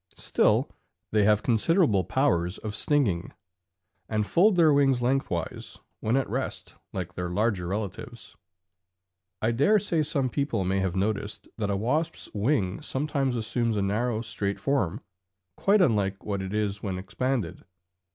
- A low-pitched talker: Yes, low, 110 Hz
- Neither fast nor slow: Yes, average, 145 wpm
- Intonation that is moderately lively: No, wide, 5.7 semitones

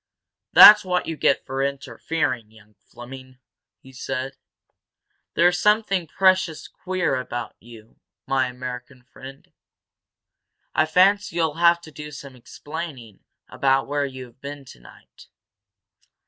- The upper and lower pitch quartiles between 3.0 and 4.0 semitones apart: No, average, 4.7 semitones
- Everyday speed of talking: No, slow, 120 wpm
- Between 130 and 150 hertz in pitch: Yes, medium, 140 Hz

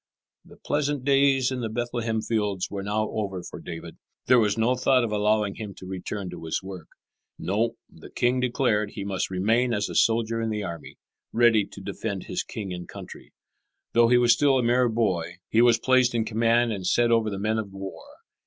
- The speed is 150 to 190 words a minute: No, fast, 205 wpm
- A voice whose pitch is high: No, low, 110 Hz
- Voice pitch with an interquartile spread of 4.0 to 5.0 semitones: No, average, 3.3 semitones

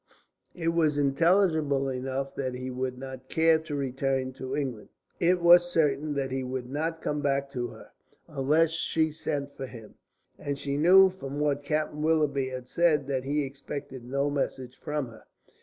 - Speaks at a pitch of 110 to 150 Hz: Yes, medium, 140 Hz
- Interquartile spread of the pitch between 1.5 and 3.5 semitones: Yes, average, 3.0 semitones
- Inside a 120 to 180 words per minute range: Yes, average, 175 wpm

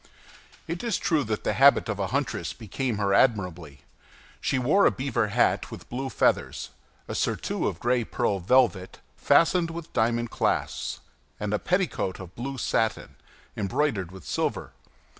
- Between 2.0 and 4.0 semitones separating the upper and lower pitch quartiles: No, wide, 5.6 semitones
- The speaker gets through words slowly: No, average, 155 wpm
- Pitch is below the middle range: Yes, low, 120 Hz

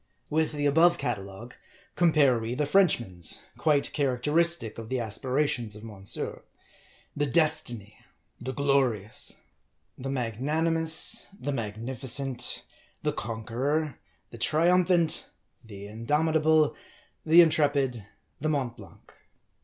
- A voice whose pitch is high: No, low, 135 Hz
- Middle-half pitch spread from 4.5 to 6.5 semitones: Yes, average, 5.1 semitones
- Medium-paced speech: No, slow, 115 wpm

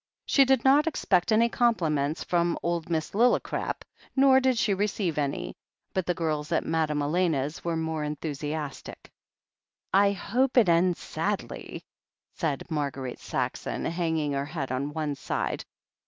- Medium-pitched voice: Yes, medium, 165 Hz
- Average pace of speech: Yes, average, 145 wpm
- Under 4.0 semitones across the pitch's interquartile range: No, average, 5.2 semitones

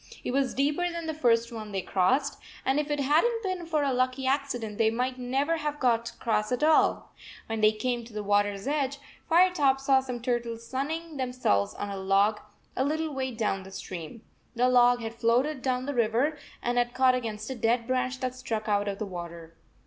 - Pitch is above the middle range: Yes, very high, 250 Hz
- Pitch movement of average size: Yes, average, 3.9 semitones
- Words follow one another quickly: Yes, fast, 220 wpm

